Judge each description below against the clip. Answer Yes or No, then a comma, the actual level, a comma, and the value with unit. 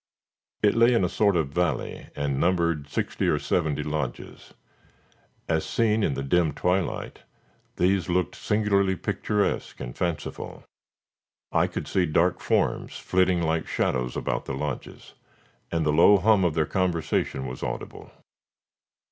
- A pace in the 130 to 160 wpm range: Yes, average, 140 wpm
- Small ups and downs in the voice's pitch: No, average, 4.0 semitones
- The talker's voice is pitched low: Yes, very low, 85 Hz